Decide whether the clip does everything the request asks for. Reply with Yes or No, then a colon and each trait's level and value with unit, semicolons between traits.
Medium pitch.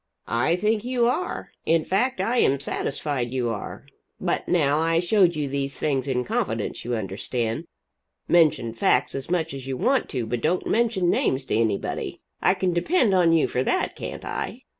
Yes: medium, 155 Hz